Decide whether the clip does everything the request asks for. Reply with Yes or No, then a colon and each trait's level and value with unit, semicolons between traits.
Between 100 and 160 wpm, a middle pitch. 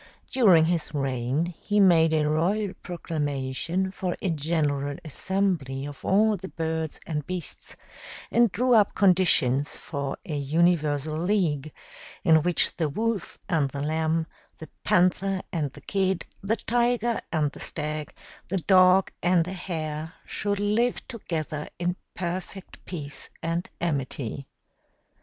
Yes: slow, 135 wpm; medium, 165 Hz